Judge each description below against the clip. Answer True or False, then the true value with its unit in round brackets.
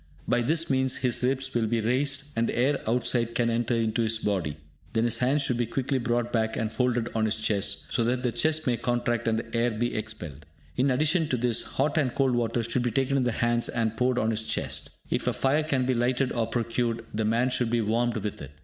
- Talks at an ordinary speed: False (240 wpm)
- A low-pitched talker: True (120 Hz)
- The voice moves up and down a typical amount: False (2.2 semitones)